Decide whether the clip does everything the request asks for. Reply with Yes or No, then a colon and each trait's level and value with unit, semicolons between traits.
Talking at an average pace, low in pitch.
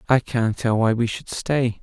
No: fast, 230 wpm; low, 115 Hz